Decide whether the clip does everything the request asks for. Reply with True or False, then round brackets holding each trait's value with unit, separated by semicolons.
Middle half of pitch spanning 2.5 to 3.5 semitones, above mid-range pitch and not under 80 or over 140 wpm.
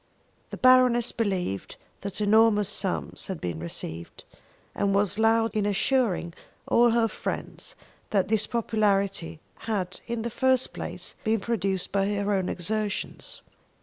True (2.8 semitones; 210 Hz; 135 wpm)